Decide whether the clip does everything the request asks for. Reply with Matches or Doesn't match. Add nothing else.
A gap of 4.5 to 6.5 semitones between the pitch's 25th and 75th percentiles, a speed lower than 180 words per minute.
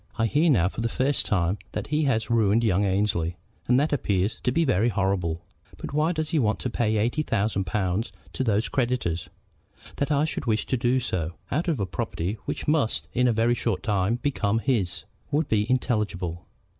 Doesn't match